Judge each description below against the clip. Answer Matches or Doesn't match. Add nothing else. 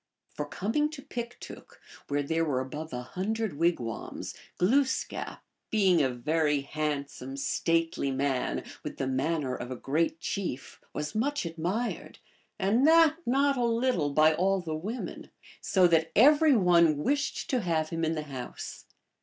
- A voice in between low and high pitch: Matches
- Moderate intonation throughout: Doesn't match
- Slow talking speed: Doesn't match